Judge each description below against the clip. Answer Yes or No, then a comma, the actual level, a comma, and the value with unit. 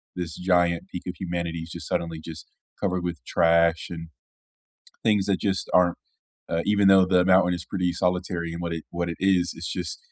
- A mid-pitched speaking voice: No, very low, 90 Hz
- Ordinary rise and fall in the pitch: No, narrow, 1.7 semitones